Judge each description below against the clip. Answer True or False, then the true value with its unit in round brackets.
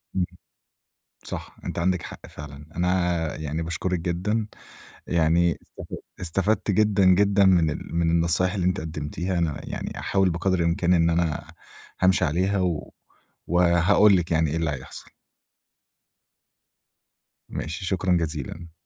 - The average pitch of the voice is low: True (85 Hz)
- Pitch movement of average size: False (2.2 semitones)